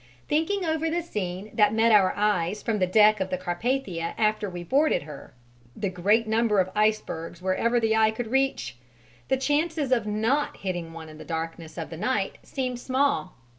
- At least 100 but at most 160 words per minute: No, average, 185 wpm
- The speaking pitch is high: Yes, high, 215 Hz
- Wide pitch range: Yes, wide, 6.0 semitones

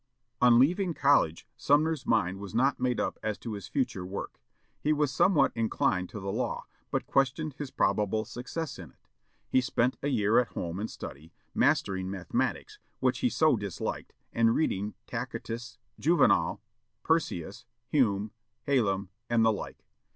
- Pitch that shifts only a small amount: No, wide, 5.6 semitones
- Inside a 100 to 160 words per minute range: Yes, average, 155 wpm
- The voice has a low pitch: Yes, low, 115 Hz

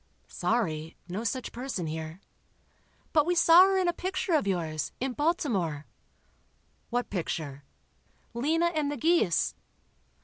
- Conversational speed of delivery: No, slow, 125 wpm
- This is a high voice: Yes, high, 240 Hz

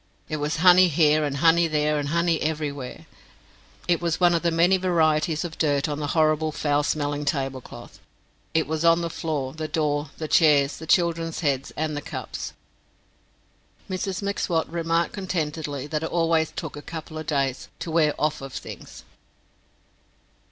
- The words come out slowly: No, average, 165 wpm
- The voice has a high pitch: No, medium, 155 Hz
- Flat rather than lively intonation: Yes, narrow, 2.2 semitones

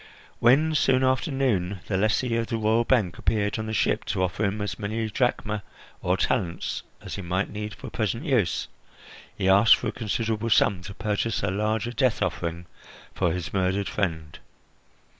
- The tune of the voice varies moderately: Yes, average, 3.5 semitones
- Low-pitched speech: Yes, low, 105 Hz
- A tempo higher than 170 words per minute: Yes, average, 180 wpm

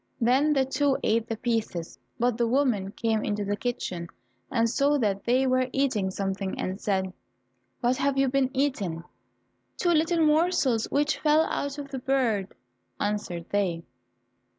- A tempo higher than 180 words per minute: No, average, 155 wpm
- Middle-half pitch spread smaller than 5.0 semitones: No, average, 5.3 semitones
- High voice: Yes, high, 245 Hz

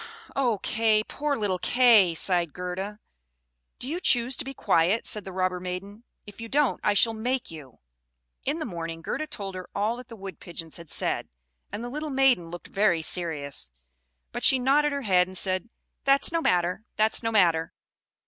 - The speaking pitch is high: Yes, high, 205 Hz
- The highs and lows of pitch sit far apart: Yes, wide, 5.7 semitones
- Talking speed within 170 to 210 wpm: Yes, average, 185 wpm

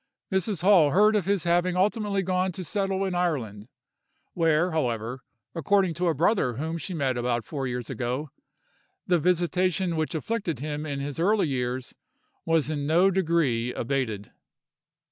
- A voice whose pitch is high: No, medium, 165 Hz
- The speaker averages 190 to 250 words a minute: No, average, 155 wpm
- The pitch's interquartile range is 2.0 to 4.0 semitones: No, wide, 5.5 semitones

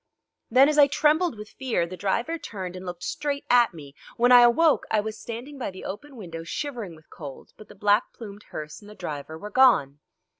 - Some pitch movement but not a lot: No, wide, 6.8 semitones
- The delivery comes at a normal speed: No, fast, 215 wpm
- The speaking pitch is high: Yes, high, 215 Hz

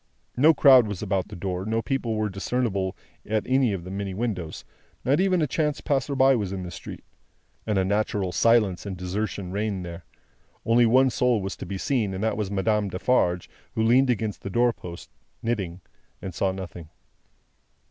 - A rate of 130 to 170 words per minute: No, average, 180 wpm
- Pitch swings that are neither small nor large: Yes, average, 4.3 semitones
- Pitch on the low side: Yes, low, 105 Hz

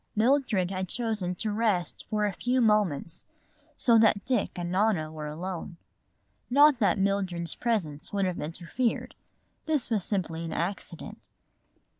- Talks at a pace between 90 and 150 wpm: Yes, average, 140 wpm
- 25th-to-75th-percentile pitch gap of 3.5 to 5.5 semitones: Yes, average, 4.5 semitones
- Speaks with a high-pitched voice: Yes, high, 195 Hz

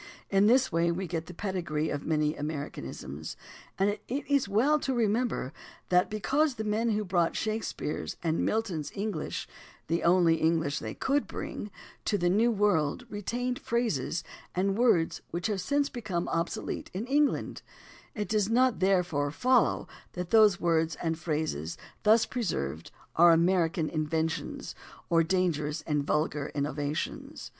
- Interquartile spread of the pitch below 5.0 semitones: No, wide, 5.5 semitones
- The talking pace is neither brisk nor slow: Yes, average, 150 wpm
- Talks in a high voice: No, medium, 180 Hz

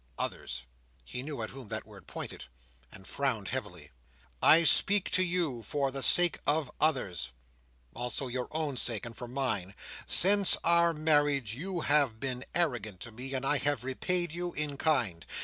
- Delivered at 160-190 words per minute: Yes, average, 165 wpm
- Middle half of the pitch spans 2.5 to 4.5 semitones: No, average, 4.9 semitones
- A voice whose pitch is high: No, low, 135 Hz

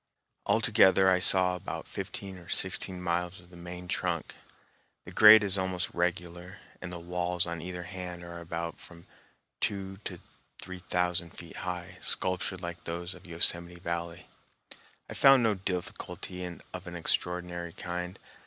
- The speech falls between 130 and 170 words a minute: Yes, average, 150 wpm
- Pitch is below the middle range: Yes, very low, 90 Hz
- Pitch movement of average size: No, narrow, 1.2 semitones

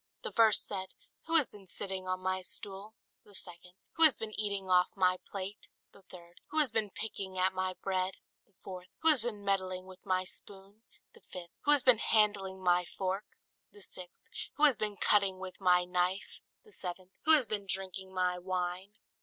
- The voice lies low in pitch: No, high, 190 Hz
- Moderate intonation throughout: No, narrow, 2.1 semitones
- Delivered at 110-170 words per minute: No, average, 195 wpm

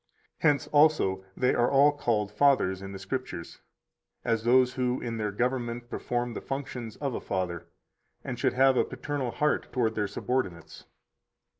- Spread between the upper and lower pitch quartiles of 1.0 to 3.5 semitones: No, average, 4.0 semitones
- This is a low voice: Yes, low, 120 Hz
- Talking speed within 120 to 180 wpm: Yes, average, 160 wpm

